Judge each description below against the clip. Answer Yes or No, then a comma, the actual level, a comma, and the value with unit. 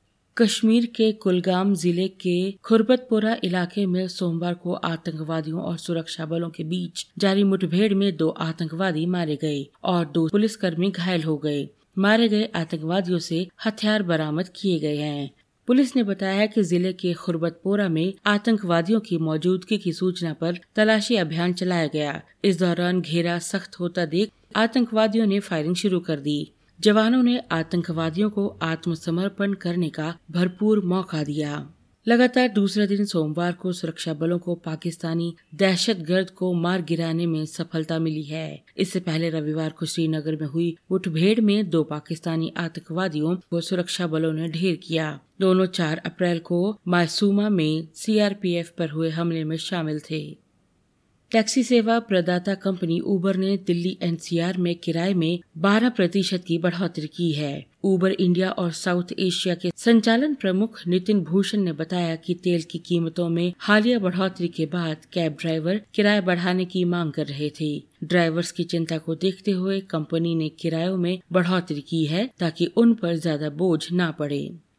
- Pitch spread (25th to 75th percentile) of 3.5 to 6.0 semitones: No, average, 2.9 semitones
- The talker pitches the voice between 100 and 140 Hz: No, medium, 175 Hz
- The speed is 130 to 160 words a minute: Yes, average, 155 wpm